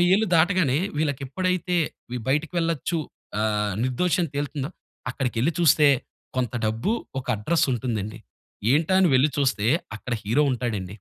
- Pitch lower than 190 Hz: Yes, medium, 140 Hz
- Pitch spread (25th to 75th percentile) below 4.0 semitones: No, wide, 5.6 semitones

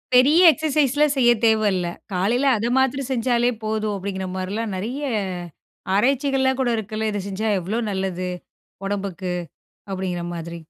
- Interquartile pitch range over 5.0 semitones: Yes, wide, 5.5 semitones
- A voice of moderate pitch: No, high, 220 Hz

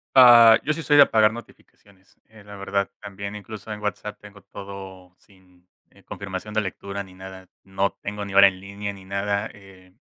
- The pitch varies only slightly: Yes, narrow, 1.6 semitones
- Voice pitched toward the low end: Yes, low, 100 Hz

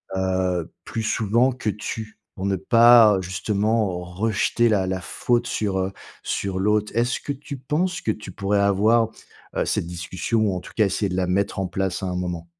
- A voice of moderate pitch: No, low, 100 Hz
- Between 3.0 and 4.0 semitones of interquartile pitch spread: Yes, average, 3.3 semitones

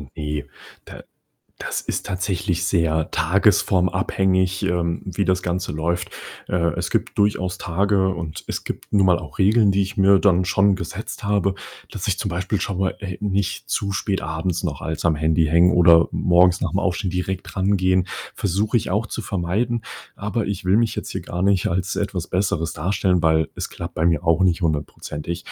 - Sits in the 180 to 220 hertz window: No, very low, 90 Hz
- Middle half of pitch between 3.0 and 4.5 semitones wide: No, narrow, 2.5 semitones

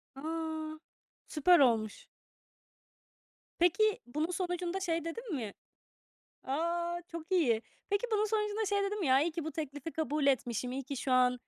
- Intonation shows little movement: No, average, 5.3 semitones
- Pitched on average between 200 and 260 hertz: No, very high, 325 Hz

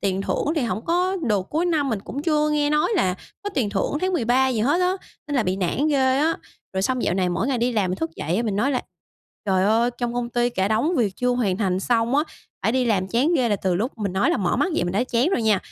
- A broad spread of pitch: Yes, wide, 6.3 semitones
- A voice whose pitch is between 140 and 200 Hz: No, high, 240 Hz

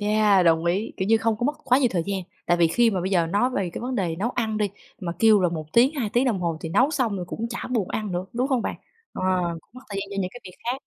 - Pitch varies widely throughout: No, average, 4.8 semitones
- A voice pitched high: Yes, high, 210 Hz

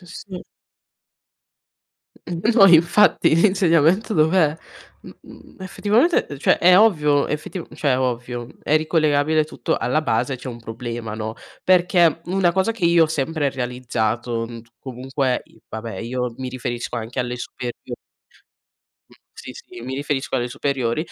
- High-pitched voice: No, medium, 145 Hz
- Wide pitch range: Yes, wide, 5.7 semitones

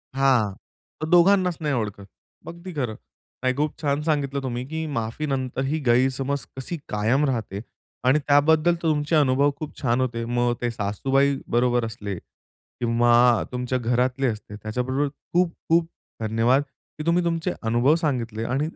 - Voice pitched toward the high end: No, low, 130 Hz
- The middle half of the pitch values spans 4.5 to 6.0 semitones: No, average, 4.0 semitones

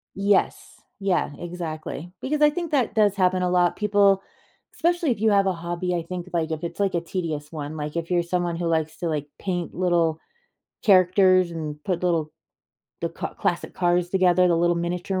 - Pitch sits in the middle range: Yes, medium, 175 Hz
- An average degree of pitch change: No, narrow, 2.2 semitones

